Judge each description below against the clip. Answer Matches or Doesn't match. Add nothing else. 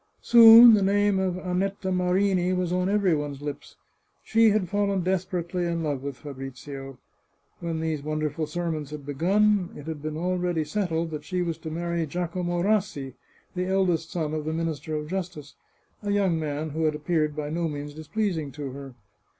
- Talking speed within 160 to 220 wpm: Matches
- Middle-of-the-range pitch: Matches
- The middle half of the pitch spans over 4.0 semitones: Doesn't match